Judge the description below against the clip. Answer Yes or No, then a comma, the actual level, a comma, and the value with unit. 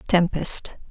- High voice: No, medium, 180 Hz